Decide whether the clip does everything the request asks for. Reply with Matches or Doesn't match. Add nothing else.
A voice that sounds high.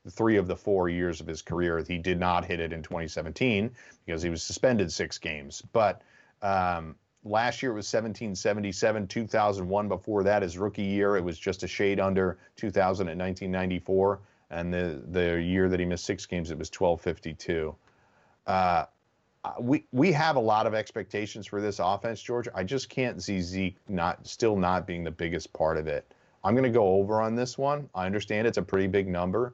Doesn't match